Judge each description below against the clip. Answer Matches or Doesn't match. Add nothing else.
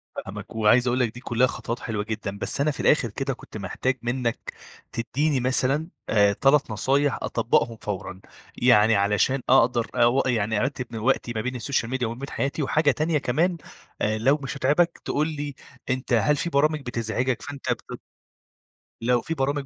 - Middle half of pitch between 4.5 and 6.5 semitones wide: Doesn't match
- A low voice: Matches